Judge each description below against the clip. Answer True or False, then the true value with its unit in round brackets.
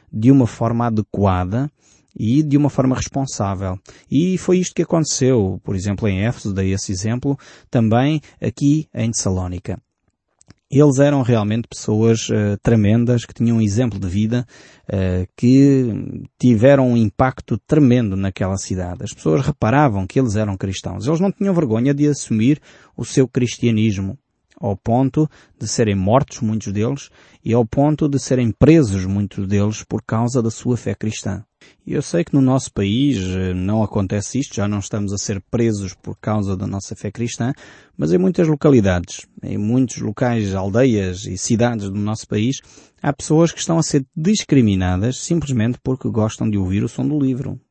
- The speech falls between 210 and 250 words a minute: False (165 wpm)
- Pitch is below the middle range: True (115 Hz)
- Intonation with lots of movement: False (4.9 semitones)